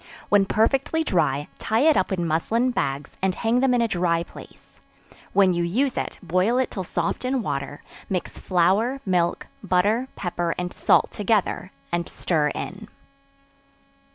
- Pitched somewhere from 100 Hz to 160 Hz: No, high, 190 Hz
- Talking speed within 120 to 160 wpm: Yes, average, 155 wpm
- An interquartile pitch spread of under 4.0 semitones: No, average, 5.2 semitones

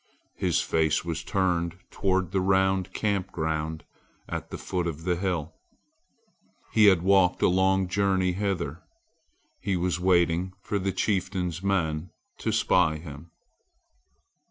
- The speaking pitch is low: Yes, very low, 90 Hz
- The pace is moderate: No, slow, 130 wpm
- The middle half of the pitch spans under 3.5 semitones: Yes, narrow, 2.4 semitones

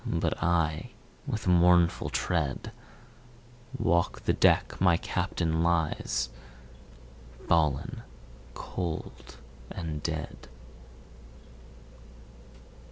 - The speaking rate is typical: No, slow, 70 wpm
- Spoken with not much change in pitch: Yes, narrow, 1.8 semitones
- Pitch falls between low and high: No, very low, 85 Hz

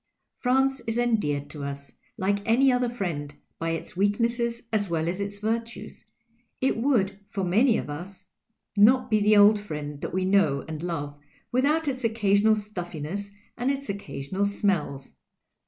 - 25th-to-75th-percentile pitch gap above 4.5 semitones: Yes, wide, 5.6 semitones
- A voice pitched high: Yes, high, 205 Hz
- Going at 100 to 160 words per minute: Yes, average, 155 wpm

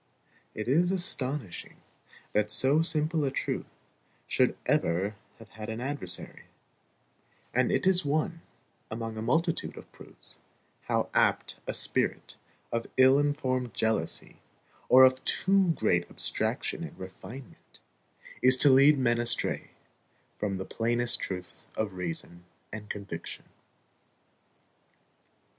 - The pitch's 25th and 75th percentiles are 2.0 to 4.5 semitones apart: No, wide, 5.4 semitones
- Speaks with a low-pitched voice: Yes, low, 120 Hz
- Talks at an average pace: No, slow, 120 wpm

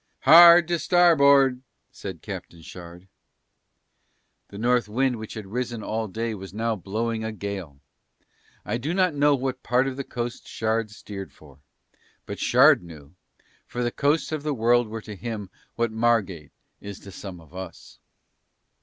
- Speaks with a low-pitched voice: Yes, low, 115 Hz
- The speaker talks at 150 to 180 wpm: Yes, average, 160 wpm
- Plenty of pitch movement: No, average, 4.7 semitones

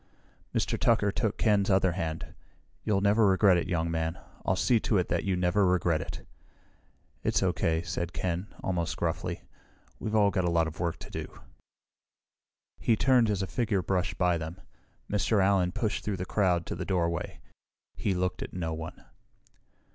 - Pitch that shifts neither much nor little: Yes, average, 3.1 semitones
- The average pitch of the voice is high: No, very low, 95 Hz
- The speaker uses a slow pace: No, average, 175 wpm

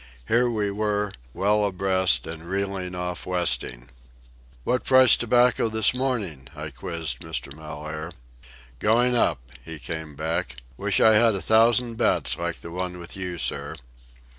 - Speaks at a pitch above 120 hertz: No, very low, 90 Hz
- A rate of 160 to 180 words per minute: No, average, 145 wpm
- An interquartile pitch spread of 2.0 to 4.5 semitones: No, wide, 5.6 semitones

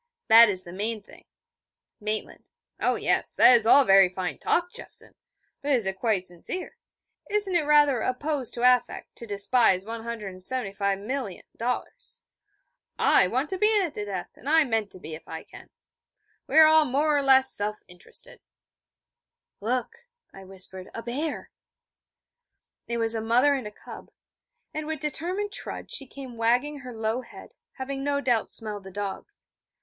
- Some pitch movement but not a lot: No, wide, 5.8 semitones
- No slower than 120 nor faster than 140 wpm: No, average, 160 wpm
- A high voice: Yes, high, 235 Hz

